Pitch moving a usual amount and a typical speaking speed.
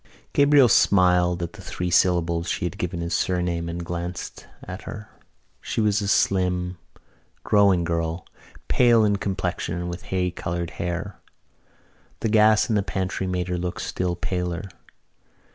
No: narrow, 2.3 semitones; average, 150 wpm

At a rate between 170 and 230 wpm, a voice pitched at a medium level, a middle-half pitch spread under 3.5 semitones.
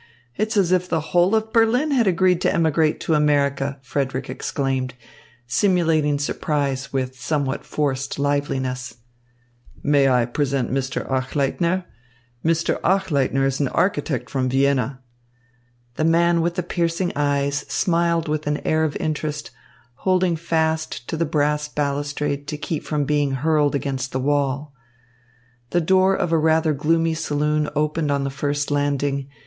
No: average, 145 wpm; medium, 150 Hz; average, 3.0 semitones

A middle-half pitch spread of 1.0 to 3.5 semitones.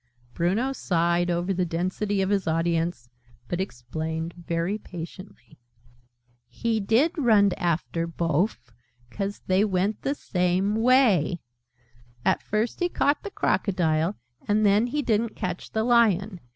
No: average, 4.2 semitones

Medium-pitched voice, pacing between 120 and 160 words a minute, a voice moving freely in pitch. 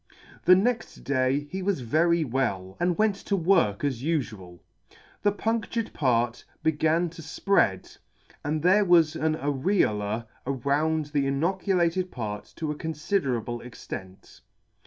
Yes: medium, 155 Hz; slow, 135 wpm; wide, 6.3 semitones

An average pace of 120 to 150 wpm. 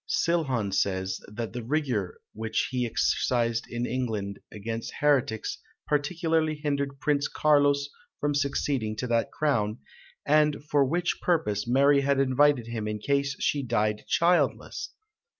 Yes: slow, 135 wpm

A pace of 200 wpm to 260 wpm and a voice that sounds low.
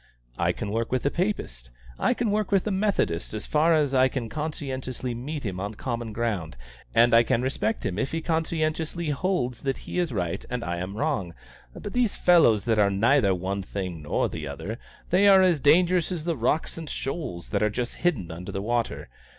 Yes: fast, 205 wpm; low, 125 Hz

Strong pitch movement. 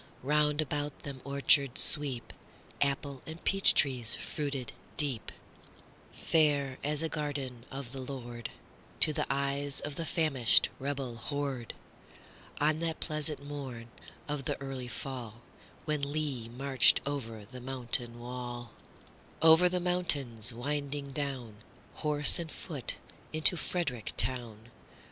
No: average, 3.1 semitones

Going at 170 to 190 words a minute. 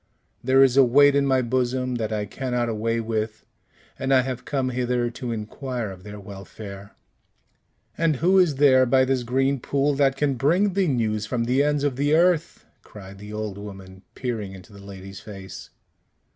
Yes: average, 185 wpm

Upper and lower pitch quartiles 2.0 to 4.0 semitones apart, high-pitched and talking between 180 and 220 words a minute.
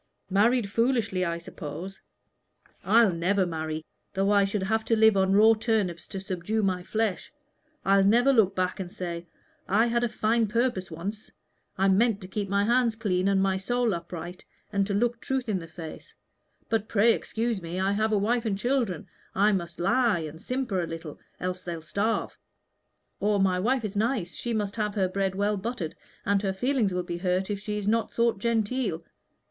Yes: average, 3.5 semitones; high, 200 Hz; average, 190 wpm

